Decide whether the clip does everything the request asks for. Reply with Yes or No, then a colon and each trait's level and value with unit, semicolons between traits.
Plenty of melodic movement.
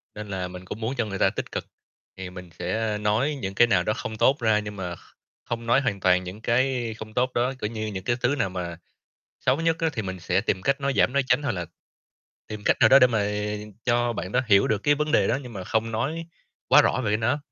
No: average, 4.6 semitones